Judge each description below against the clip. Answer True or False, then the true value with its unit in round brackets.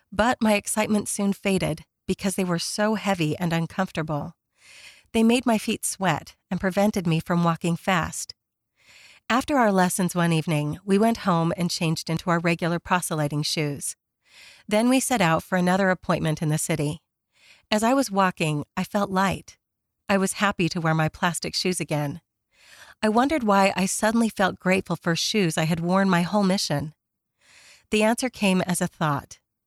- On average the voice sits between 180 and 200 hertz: True (185 Hz)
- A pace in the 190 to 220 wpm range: False (170 wpm)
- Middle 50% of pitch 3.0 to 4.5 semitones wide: True (3.8 semitones)